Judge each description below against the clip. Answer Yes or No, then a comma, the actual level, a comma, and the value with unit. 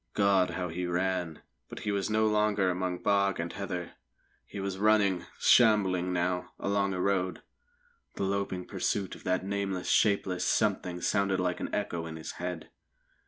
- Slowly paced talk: No, average, 165 wpm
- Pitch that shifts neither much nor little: No, narrow, 1.8 semitones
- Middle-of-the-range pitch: No, very low, 95 Hz